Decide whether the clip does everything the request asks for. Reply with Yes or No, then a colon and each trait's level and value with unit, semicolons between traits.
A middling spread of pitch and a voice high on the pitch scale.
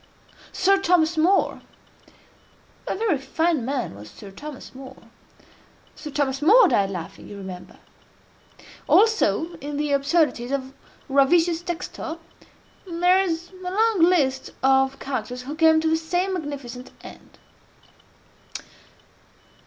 Yes: average, 4.8 semitones; very high, 300 Hz